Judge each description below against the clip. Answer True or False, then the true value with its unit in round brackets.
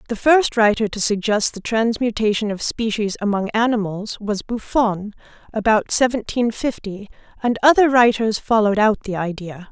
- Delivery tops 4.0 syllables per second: True (4.9 syllables/s)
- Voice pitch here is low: False (220 Hz)